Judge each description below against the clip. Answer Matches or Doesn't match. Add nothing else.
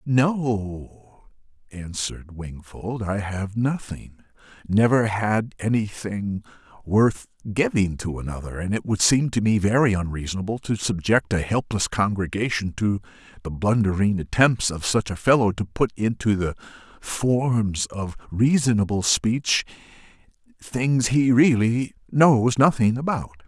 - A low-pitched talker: Matches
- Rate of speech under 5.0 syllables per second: Matches